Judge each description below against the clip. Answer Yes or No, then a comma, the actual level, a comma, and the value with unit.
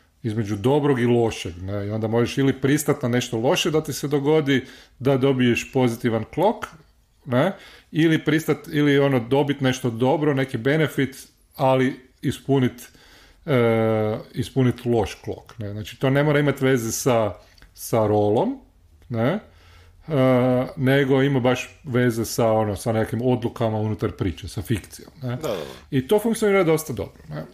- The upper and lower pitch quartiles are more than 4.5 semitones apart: No, average, 3.8 semitones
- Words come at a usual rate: Yes, average, 150 wpm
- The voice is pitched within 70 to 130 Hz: Yes, low, 125 Hz